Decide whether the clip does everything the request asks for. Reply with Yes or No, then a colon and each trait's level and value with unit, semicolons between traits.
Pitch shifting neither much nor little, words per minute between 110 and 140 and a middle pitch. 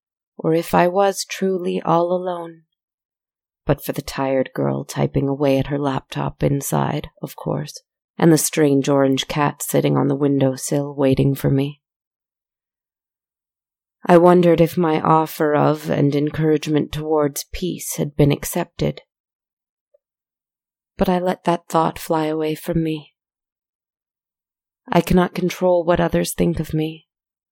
Yes: average, 3.7 semitones; slow, 135 wpm; medium, 155 Hz